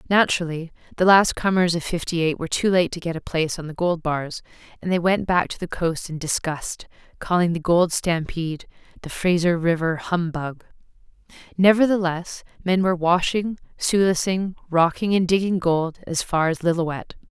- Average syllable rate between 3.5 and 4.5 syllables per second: No, 5.0 syllables/s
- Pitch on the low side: No, medium, 175 Hz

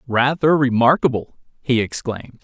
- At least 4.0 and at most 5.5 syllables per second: Yes, 5.2 syllables/s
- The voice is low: Yes, low, 130 Hz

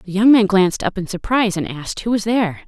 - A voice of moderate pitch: No, high, 200 Hz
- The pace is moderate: No, fast, 270 wpm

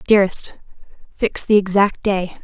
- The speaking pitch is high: Yes, high, 195 Hz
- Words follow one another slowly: Yes, slow, 125 wpm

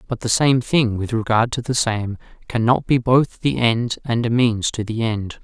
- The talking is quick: Yes, fast, 220 wpm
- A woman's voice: No, male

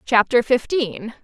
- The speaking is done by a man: No, female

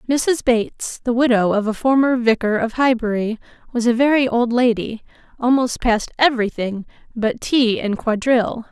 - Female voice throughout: Yes, female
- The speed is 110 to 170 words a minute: Yes, average, 160 wpm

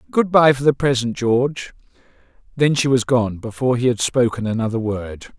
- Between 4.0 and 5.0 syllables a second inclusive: No, 5.4 syllables/s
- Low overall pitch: Yes, low, 120 Hz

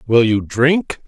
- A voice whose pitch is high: No, low, 130 Hz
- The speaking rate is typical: Yes, average, 165 wpm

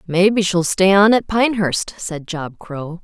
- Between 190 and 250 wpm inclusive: No, average, 180 wpm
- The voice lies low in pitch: No, medium, 185 Hz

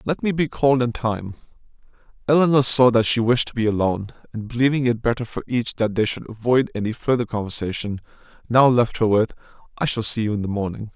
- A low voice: Yes, low, 115 Hz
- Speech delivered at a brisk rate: Yes, fast, 210 wpm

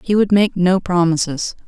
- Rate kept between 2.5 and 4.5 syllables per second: No, 4.7 syllables/s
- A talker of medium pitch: Yes, medium, 180 Hz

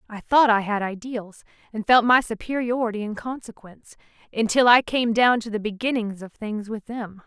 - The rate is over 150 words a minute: Yes, average, 180 wpm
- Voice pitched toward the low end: No, high, 225 Hz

